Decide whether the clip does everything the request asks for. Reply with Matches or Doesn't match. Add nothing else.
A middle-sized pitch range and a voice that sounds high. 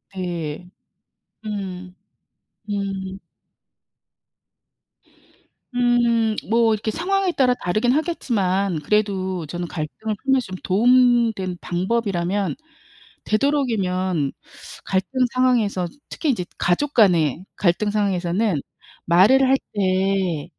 Matches